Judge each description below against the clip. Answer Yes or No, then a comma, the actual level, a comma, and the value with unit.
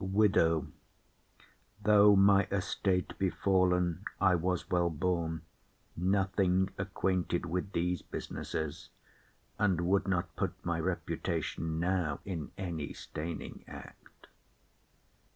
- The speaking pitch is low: Yes, very low, 90 Hz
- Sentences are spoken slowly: Yes, slow, 100 wpm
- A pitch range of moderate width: No, narrow, 2.3 semitones